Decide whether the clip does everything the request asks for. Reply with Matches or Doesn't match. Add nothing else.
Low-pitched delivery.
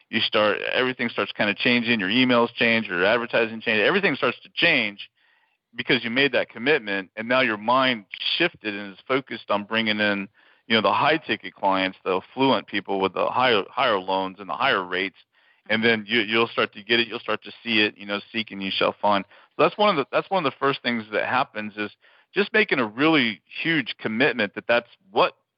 Matches